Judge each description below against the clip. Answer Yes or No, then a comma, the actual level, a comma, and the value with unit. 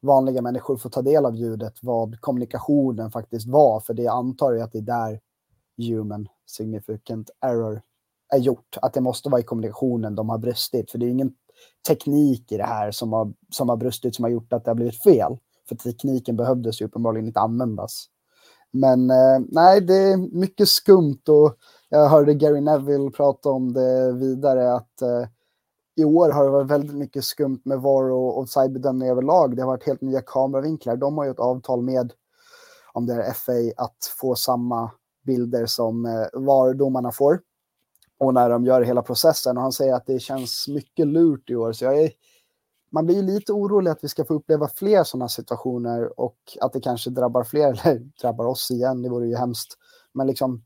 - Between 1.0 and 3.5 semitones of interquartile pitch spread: Yes, average, 3.1 semitones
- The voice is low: Yes, low, 130 Hz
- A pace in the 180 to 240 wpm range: Yes, fast, 195 wpm